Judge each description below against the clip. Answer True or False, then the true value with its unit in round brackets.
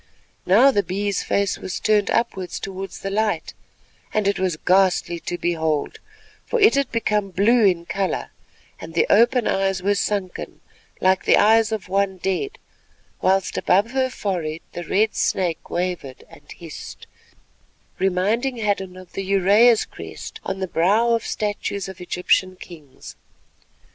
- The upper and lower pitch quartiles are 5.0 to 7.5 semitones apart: False (2.8 semitones)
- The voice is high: True (195 Hz)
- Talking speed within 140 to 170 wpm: True (150 wpm)